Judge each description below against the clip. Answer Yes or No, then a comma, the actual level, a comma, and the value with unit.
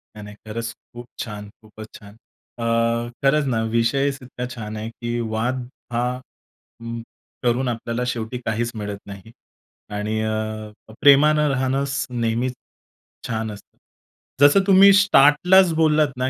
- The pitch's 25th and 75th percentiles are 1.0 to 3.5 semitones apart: No, average, 4.0 semitones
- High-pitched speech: No, low, 120 Hz